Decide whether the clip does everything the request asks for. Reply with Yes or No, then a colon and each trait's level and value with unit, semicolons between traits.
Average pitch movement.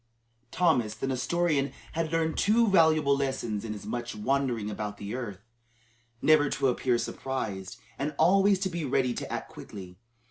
No: wide, 6.4 semitones